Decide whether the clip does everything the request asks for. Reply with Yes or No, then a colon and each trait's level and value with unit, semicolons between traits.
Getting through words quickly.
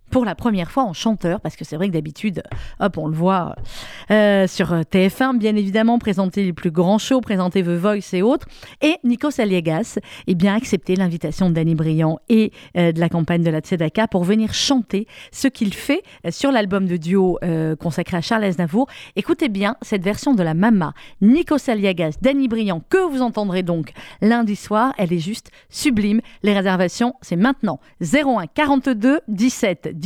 No: average, 190 wpm